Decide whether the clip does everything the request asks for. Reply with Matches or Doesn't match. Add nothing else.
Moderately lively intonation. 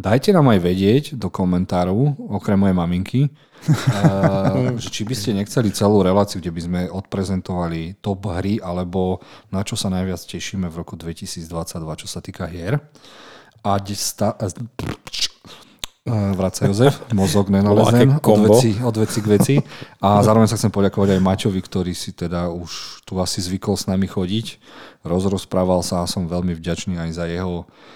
Matches